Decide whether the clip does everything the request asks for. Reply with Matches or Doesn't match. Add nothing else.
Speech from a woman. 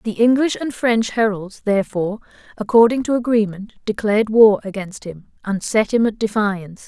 Matches